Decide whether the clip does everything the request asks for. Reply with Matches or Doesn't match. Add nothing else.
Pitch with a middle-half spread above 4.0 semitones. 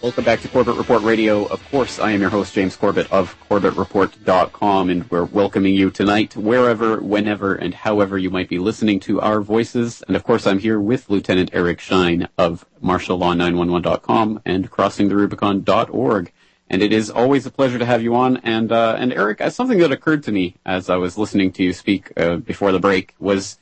Doesn't match